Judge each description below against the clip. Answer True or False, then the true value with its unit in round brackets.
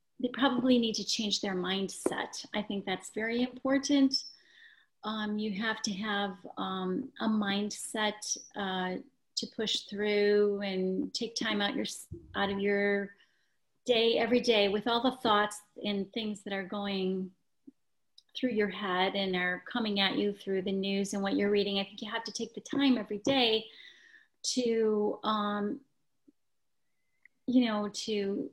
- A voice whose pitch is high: True (210 Hz)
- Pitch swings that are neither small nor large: True (3.3 semitones)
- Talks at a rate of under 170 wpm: True (155 wpm)